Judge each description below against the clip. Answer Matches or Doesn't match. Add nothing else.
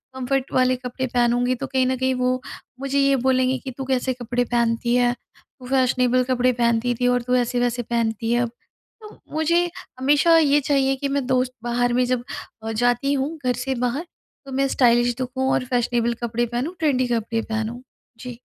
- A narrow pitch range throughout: Matches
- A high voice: Matches